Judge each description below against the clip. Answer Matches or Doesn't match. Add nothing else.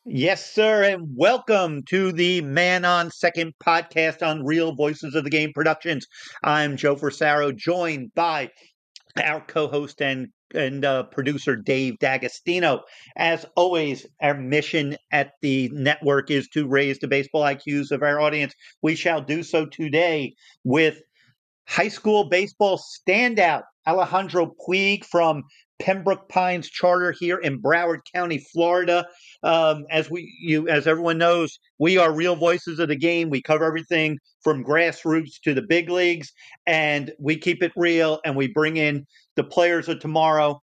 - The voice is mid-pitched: Matches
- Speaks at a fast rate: Doesn't match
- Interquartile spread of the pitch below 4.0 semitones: Matches